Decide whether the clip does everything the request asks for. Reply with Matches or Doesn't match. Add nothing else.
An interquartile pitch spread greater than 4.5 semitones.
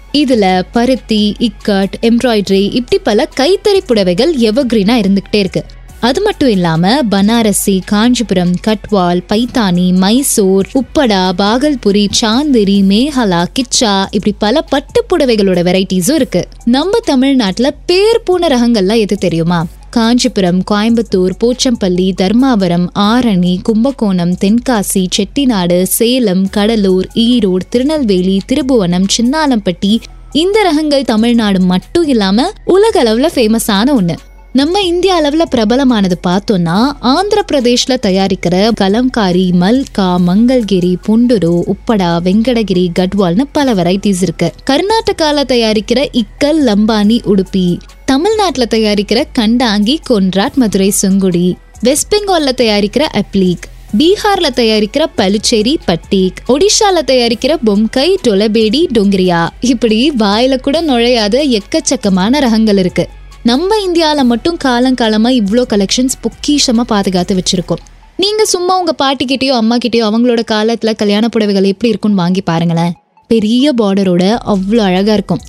Matches